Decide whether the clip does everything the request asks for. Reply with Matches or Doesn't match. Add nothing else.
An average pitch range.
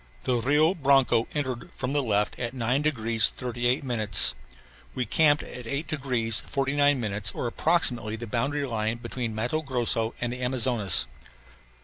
Matches